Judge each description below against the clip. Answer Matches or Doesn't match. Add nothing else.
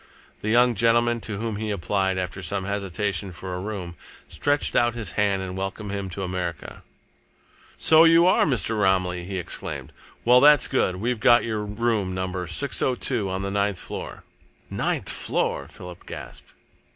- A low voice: Matches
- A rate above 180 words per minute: Doesn't match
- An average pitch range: Matches